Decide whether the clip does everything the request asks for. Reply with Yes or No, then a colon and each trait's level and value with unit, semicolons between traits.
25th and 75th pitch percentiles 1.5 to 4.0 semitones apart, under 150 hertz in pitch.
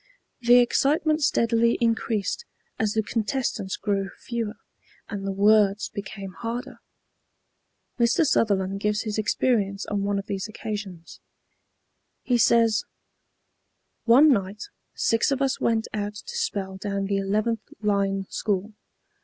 No: average, 2.9 semitones; high, 215 Hz